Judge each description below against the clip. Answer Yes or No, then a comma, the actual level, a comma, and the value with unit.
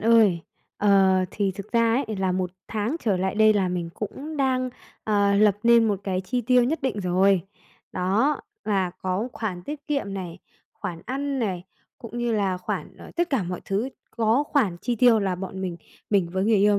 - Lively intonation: No, average, 3.9 semitones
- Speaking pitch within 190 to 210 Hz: Yes, high, 205 Hz